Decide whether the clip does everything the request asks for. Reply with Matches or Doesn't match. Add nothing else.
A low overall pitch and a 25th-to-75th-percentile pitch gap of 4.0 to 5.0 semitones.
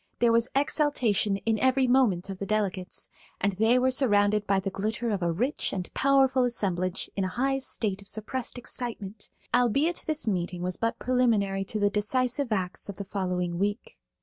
Doesn't match